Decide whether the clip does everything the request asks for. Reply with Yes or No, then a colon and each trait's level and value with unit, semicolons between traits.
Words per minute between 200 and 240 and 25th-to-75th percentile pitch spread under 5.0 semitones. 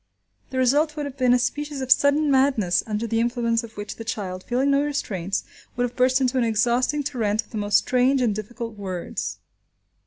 Yes: fast, 205 wpm; average, 3.8 semitones